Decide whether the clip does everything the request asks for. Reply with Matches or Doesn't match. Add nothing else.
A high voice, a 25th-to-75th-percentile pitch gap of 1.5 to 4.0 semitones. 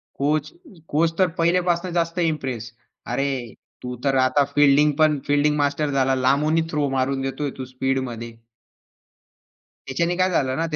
Doesn't match